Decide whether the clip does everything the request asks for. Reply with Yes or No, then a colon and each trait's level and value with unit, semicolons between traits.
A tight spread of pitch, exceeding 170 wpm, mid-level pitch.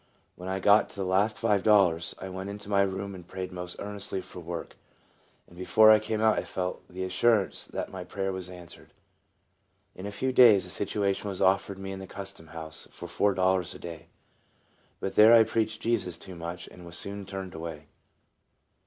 No: narrow, 2.1 semitones; average, 200 wpm; very low, 95 Hz